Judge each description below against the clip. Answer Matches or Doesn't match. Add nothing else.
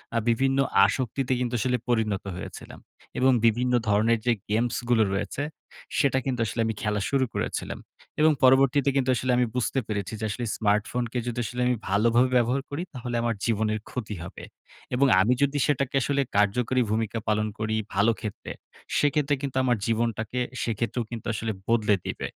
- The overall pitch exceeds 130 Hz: Doesn't match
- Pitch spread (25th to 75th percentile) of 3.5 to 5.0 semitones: Doesn't match